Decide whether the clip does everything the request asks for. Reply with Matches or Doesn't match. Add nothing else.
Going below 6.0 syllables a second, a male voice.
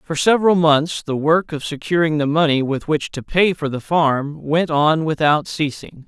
Matches